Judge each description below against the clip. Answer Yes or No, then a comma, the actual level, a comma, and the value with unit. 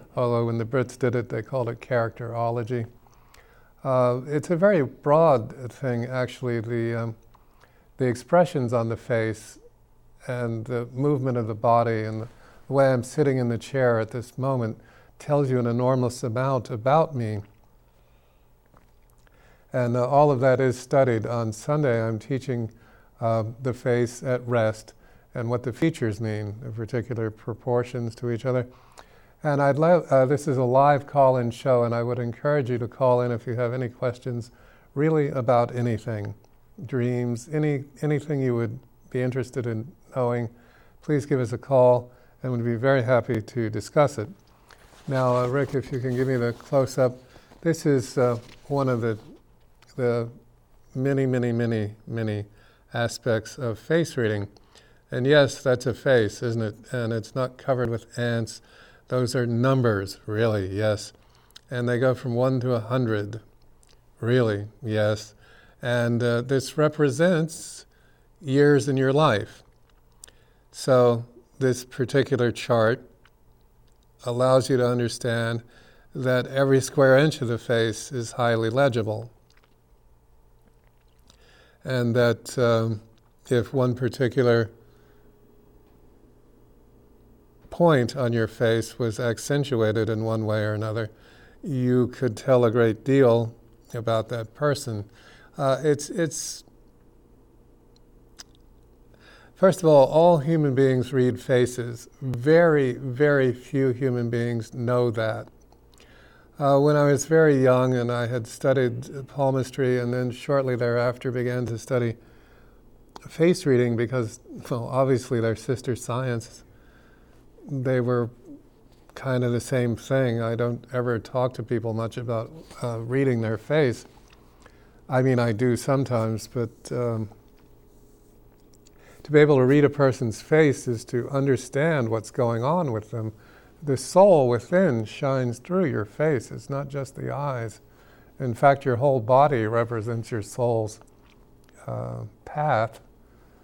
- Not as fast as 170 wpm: Yes, average, 140 wpm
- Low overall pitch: Yes, low, 120 Hz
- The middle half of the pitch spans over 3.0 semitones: No, narrow, 2.6 semitones